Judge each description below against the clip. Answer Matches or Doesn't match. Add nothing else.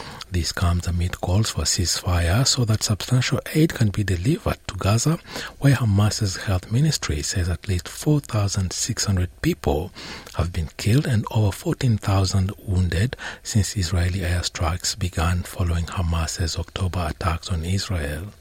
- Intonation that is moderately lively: Matches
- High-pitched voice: Doesn't match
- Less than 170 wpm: Matches